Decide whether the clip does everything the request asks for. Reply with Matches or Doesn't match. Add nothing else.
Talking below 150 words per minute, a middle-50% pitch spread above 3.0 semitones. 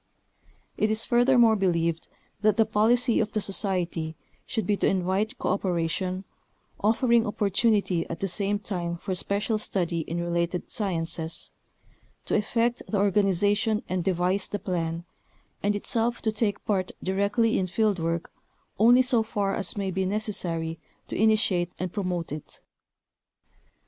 Matches